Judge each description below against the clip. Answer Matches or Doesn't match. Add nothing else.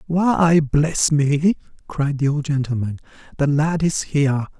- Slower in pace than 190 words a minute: Matches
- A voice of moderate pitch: Matches